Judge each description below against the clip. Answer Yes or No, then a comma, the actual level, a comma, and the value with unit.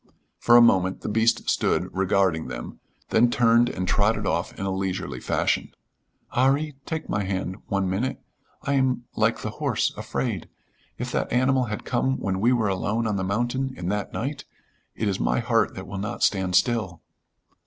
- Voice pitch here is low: Yes, low, 105 Hz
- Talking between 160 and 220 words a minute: Yes, average, 180 wpm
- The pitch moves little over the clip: No, average, 4.2 semitones